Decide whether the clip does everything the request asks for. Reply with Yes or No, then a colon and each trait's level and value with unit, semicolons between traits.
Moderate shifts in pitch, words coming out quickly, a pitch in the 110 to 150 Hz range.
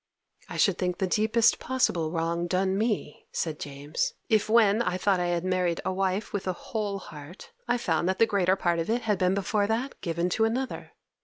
No: average, 3.7 semitones; fast, 210 wpm; high, 190 Hz